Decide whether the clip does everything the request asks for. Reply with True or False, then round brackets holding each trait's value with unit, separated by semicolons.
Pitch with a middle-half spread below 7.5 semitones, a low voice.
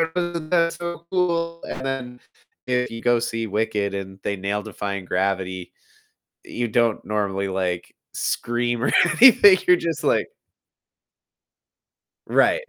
False (9.0 semitones; 120 Hz)